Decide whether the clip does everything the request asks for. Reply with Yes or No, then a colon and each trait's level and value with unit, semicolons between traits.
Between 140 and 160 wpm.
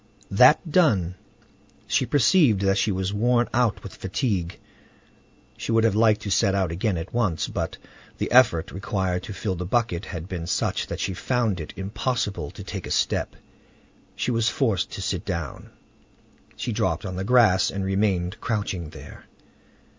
No: average, 170 wpm